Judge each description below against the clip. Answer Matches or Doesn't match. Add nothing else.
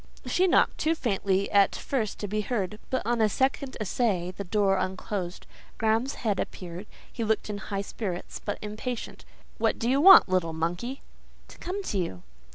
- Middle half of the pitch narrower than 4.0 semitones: Doesn't match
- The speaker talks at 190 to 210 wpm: Doesn't match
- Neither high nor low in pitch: Doesn't match